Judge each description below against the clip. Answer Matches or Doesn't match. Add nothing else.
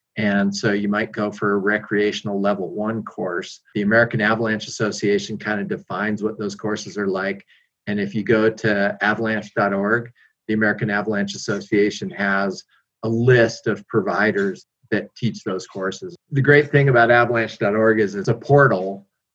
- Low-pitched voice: Matches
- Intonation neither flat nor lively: Doesn't match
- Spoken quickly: Doesn't match